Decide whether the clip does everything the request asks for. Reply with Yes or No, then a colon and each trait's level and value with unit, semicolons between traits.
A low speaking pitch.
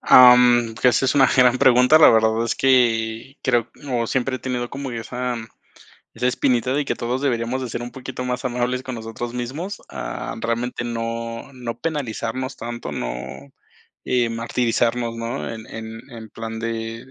Yes: low, 120 Hz